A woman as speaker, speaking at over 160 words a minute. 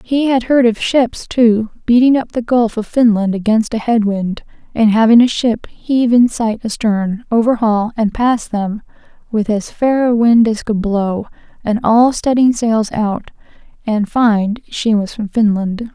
Yes: female; average, 175 wpm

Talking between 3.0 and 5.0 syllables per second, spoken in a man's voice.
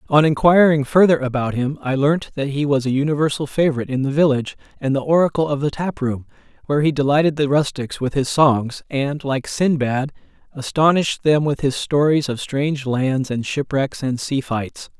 No: 5.3 syllables/s; male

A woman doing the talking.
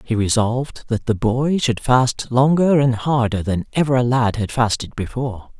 No: male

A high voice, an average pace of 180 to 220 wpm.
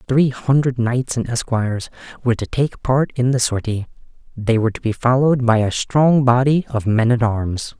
No: low, 120 Hz; average, 190 wpm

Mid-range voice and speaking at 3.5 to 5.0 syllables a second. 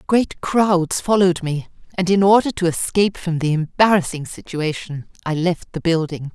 Yes: medium, 175 Hz; 4.8 syllables/s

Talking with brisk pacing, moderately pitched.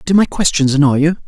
Yes: fast, 235 wpm; medium, 155 Hz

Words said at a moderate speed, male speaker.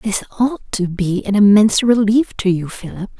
No: average, 190 wpm; female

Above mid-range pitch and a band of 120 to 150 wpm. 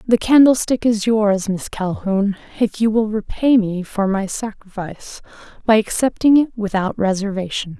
Yes: high, 210 Hz; average, 140 wpm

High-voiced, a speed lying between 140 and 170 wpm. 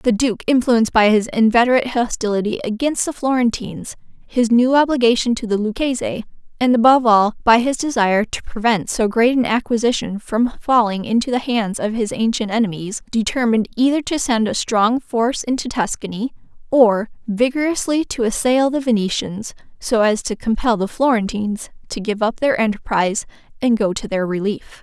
Yes: high, 230 Hz; average, 165 wpm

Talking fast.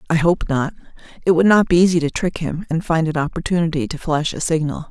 Yes: fast, 235 wpm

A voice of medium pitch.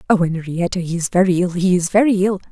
Yes: medium, 180 Hz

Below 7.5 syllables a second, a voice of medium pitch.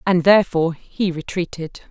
Yes: 5.3 syllables/s; medium, 175 Hz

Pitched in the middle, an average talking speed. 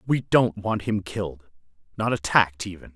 No: low, 100 Hz; average, 160 wpm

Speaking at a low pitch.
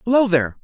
No: high, 190 Hz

